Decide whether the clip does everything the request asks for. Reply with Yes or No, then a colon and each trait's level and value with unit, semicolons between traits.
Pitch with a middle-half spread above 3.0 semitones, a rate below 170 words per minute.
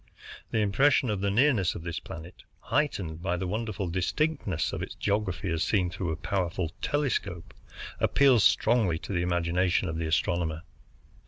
Yes: average, 4.0 semitones; average, 160 wpm